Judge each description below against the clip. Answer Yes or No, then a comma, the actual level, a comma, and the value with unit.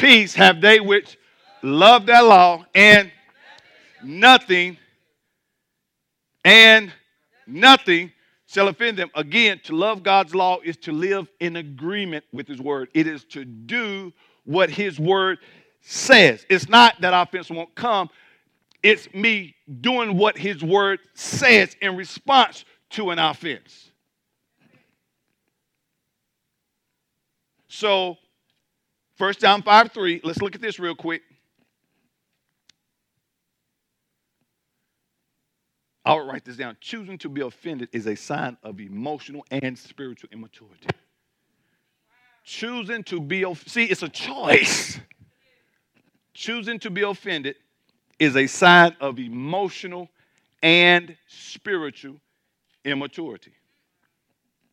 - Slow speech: Yes, slow, 110 wpm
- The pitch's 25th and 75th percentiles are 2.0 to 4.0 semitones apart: No, average, 4.7 semitones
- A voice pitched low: No, medium, 185 Hz